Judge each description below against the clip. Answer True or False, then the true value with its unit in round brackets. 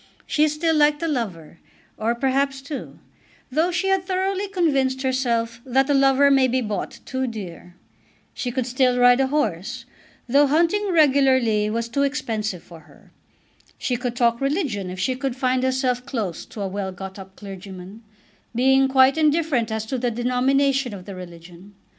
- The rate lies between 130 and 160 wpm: False (170 wpm)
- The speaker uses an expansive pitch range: False (4.3 semitones)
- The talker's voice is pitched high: True (255 Hz)